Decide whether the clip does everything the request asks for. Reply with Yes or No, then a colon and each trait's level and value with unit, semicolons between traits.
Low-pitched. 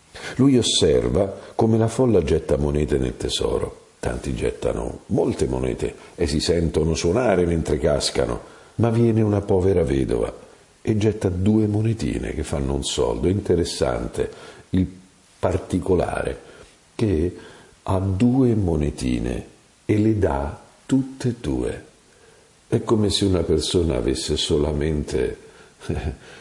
Yes: very low, 95 Hz